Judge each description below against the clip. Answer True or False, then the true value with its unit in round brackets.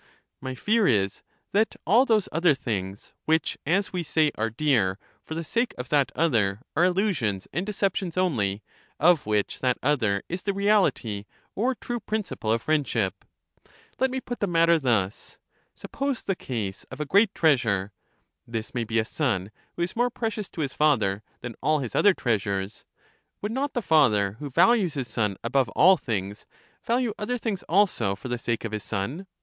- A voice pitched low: False (150 Hz)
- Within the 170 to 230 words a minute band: True (180 wpm)